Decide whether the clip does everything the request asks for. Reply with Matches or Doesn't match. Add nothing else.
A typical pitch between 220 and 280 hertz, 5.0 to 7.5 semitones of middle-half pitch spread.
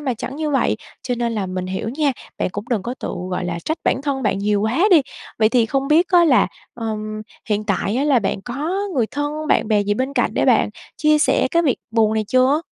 Matches